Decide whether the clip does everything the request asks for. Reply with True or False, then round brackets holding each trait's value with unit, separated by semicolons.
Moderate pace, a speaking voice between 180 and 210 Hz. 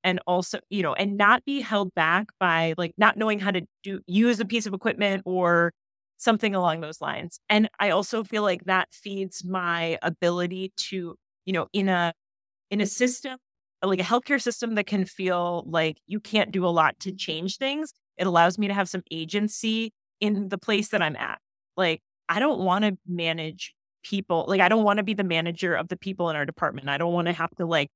False (215 wpm; 190 Hz)